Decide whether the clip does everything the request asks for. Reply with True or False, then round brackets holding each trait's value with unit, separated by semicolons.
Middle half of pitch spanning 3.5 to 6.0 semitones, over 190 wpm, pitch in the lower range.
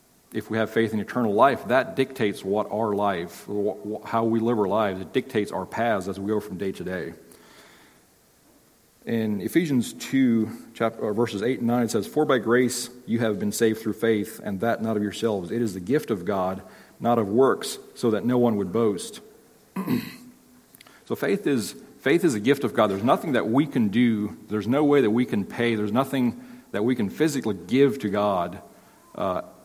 True (4.2 semitones; 200 wpm; 115 Hz)